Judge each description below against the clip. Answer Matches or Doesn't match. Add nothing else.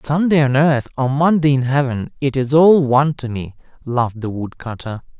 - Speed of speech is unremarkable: Matches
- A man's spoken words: Matches